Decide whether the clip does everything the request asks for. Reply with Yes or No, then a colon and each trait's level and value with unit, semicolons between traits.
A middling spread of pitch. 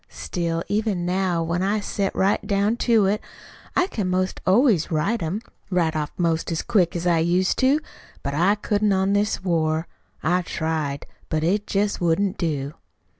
Yes: average, 3.7 semitones